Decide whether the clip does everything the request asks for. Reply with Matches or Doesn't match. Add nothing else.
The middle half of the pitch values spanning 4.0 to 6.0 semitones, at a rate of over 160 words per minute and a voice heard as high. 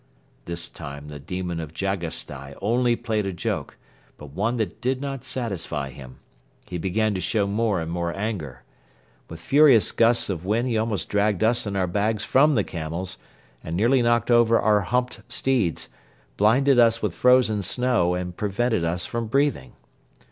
Doesn't match